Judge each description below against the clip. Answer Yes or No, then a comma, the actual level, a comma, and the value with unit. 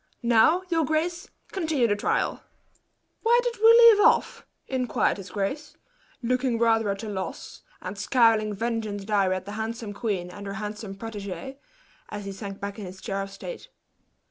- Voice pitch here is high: Yes, high, 220 Hz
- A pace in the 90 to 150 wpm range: No, average, 170 wpm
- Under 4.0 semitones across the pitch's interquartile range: No, average, 5.2 semitones